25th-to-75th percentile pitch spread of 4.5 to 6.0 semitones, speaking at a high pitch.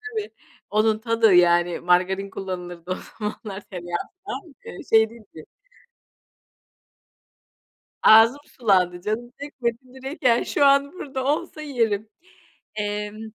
Yes: wide, 5.6 semitones; high, 220 Hz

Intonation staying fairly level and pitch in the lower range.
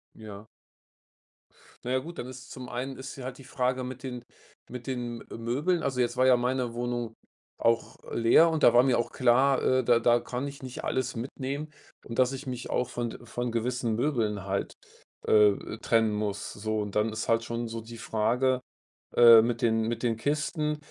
Yes: narrow, 2.2 semitones; low, 120 Hz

